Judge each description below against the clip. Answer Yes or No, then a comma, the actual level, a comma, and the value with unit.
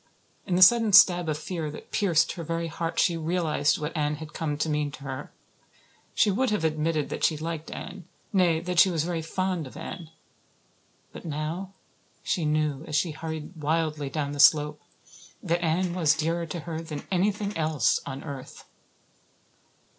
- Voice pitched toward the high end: No, medium, 160 Hz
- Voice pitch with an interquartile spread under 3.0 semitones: Yes, narrow, 2.6 semitones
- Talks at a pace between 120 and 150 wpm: No, average, 175 wpm